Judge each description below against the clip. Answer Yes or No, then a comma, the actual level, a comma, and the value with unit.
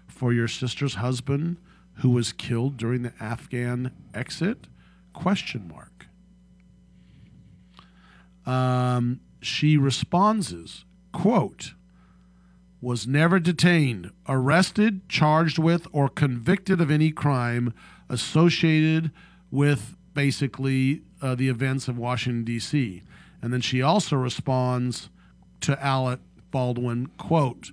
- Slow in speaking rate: Yes, slow, 100 wpm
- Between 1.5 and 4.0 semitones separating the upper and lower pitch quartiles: No, average, 4.7 semitones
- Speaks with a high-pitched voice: No, low, 130 Hz